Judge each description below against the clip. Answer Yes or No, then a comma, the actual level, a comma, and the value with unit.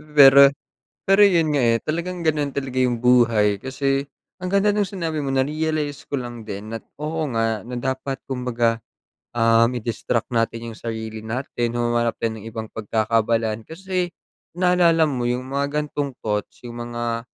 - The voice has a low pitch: Yes, low, 125 Hz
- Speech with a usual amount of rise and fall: Yes, average, 4.7 semitones